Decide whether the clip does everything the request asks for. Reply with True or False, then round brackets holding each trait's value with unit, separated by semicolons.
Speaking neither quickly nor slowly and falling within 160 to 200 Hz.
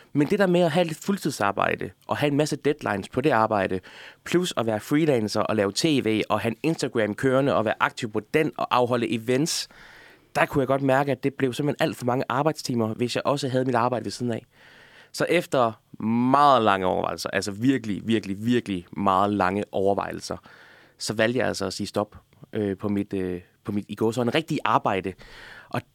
False (210 wpm; 115 Hz)